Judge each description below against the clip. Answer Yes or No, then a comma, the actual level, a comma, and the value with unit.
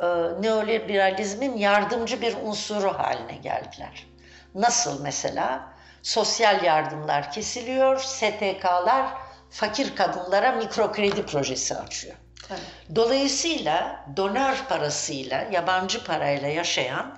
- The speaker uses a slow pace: Yes, slow, 80 wpm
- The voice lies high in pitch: Yes, high, 205 Hz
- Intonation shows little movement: No, wide, 5.6 semitones